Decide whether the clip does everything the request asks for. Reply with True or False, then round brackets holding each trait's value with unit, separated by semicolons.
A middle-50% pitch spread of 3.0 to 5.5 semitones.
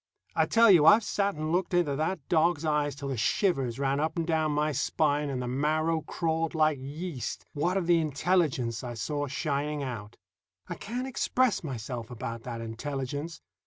True (3.8 semitones)